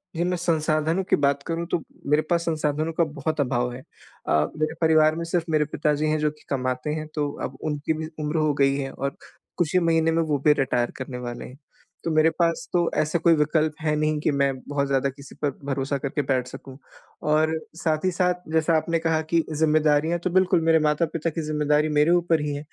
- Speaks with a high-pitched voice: No, medium, 155 Hz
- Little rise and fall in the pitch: Yes, narrow, 2.3 semitones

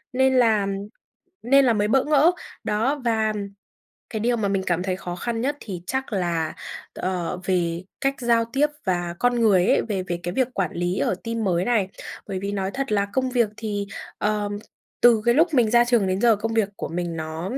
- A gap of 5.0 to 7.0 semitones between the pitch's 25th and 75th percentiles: No, average, 4.5 semitones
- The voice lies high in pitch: Yes, high, 210 Hz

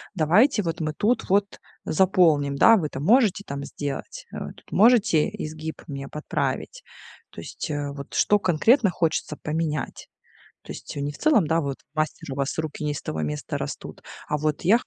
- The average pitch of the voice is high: No, medium, 155 Hz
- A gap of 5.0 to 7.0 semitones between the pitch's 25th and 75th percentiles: Yes, wide, 5.4 semitones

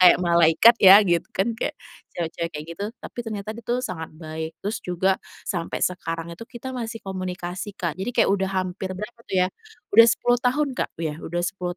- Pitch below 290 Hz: Yes, medium, 185 Hz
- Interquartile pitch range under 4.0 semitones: No, average, 4.6 semitones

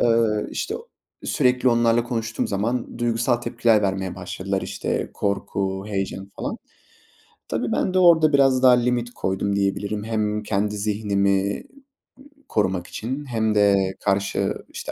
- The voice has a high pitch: No, low, 110 Hz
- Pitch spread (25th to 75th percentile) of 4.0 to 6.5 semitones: No, average, 3.2 semitones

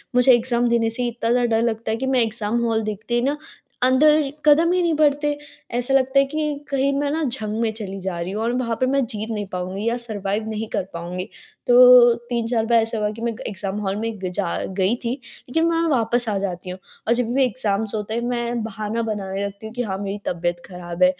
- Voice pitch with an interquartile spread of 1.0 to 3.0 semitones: No, average, 3.4 semitones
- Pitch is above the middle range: Yes, high, 230 Hz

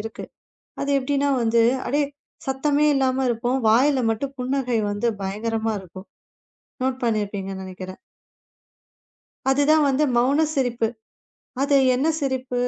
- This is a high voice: Yes, very high, 250 Hz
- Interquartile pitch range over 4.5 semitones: No, average, 3.8 semitones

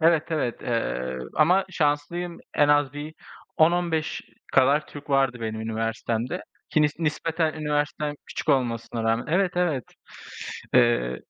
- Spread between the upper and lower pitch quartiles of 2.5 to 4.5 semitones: No, average, 5.1 semitones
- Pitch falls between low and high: Yes, medium, 145 Hz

